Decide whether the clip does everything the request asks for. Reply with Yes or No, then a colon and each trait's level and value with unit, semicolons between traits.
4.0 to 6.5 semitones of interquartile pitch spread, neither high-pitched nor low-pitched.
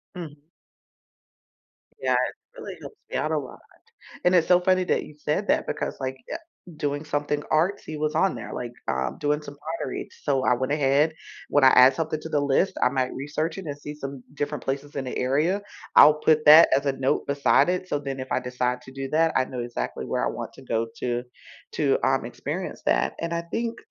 No: average, 3.0 semitones; medium, 145 Hz